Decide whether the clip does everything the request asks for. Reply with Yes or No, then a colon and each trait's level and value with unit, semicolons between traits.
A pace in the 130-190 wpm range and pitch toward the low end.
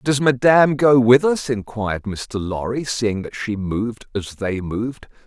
Yes: average, 170 wpm; low, 115 Hz